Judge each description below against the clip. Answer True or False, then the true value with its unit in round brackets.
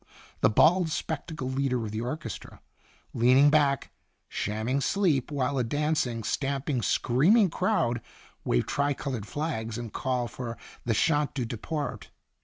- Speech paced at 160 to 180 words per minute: False (145 wpm)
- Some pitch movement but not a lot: True (4.1 semitones)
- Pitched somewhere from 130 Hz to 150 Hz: True (135 Hz)